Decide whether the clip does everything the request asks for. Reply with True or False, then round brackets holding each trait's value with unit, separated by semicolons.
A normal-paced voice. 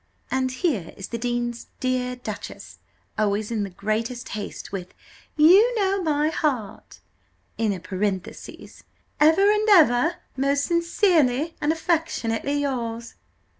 False (125 wpm)